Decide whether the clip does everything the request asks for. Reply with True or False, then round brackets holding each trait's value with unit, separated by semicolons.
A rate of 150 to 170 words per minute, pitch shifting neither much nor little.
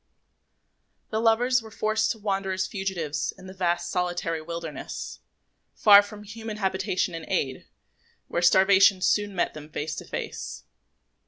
True (155 wpm; 3.4 semitones)